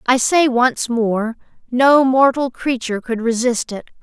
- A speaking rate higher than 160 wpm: No, average, 150 wpm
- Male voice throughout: No, female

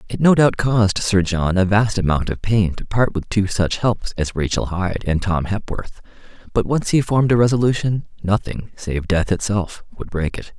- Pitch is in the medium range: No, low, 100 Hz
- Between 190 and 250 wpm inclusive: Yes, fast, 205 wpm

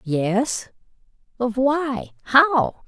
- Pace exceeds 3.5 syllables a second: No, 2.5 syllables/s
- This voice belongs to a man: No, female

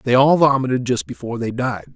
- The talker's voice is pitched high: No, low, 125 Hz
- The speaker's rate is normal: No, fast, 215 wpm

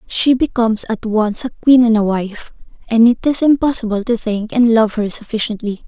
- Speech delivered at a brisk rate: No, average, 195 wpm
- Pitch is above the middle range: Yes, high, 225 Hz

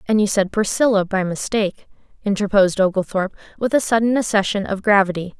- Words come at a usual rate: Yes, average, 155 wpm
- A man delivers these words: No, female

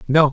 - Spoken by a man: Yes, male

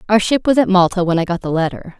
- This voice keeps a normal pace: No, fast, 300 wpm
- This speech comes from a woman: Yes, female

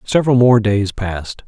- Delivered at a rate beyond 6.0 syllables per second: No, 5.1 syllables/s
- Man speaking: Yes, male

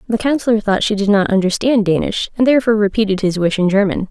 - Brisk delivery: Yes, fast, 220 wpm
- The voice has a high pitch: Yes, high, 205 Hz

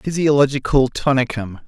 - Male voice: Yes, male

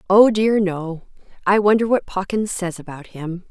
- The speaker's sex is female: Yes, female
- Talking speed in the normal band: Yes, average, 170 wpm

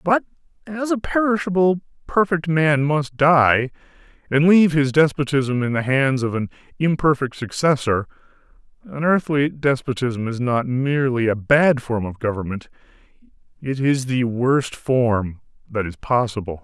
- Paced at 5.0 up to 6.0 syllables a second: No, 4.5 syllables/s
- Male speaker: Yes, male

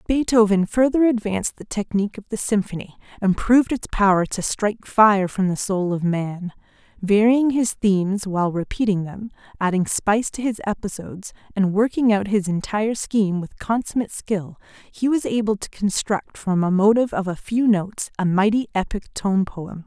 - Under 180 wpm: Yes, average, 170 wpm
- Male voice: No, female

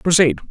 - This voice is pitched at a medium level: Yes, medium, 145 Hz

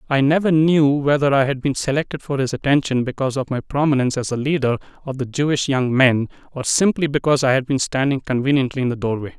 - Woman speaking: No, male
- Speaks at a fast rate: Yes, fast, 215 wpm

